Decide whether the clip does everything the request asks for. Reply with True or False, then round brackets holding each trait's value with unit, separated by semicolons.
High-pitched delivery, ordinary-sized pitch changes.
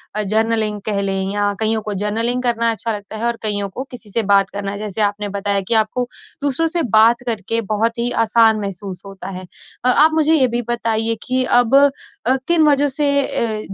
True (225 Hz; 3.2 semitones)